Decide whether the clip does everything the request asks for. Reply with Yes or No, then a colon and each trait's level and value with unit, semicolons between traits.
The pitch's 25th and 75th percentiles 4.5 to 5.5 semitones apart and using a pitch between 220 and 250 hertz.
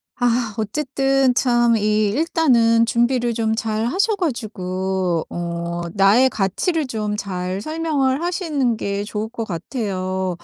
Yes: average, 5.1 semitones; high, 230 Hz